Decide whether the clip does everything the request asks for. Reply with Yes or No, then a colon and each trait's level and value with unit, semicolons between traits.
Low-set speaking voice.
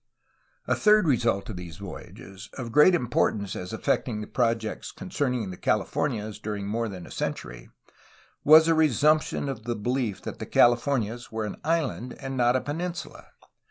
Yes: low, 120 Hz